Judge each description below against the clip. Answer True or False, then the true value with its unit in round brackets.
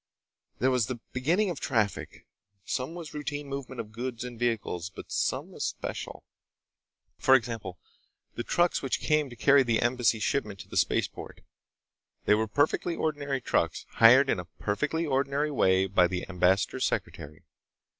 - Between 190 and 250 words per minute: False (155 wpm)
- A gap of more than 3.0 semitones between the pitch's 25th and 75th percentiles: True (5.1 semitones)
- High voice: False (125 Hz)